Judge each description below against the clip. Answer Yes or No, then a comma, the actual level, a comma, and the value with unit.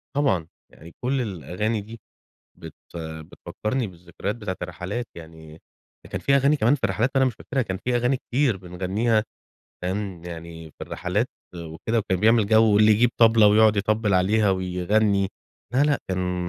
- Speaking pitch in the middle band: No, low, 105 Hz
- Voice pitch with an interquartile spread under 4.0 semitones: No, average, 4.3 semitones